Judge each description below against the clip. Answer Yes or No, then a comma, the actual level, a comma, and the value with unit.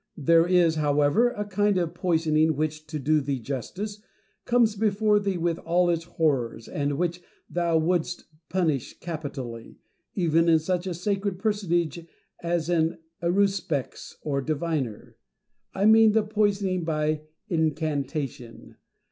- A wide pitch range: No, average, 3.8 semitones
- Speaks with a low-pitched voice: No, medium, 170 Hz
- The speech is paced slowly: Yes, slow, 130 wpm